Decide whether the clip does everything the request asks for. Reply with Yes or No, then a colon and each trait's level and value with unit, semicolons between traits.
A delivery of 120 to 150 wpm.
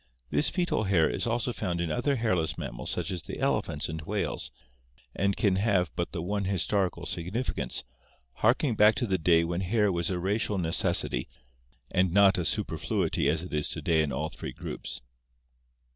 No: average, 185 wpm